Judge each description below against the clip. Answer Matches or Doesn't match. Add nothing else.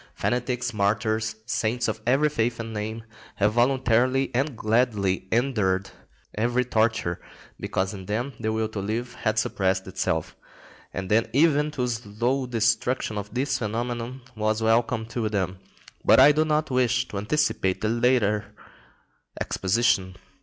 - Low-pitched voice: Matches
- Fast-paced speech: Doesn't match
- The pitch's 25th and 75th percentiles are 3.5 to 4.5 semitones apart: Doesn't match